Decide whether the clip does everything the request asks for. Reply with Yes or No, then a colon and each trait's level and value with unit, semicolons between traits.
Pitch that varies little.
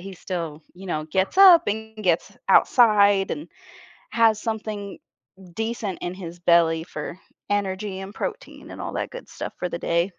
No: average, 3.8 semitones